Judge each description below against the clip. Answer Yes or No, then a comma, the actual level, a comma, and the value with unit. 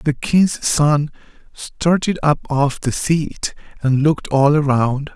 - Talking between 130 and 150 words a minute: Yes, average, 140 wpm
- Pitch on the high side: No, medium, 145 Hz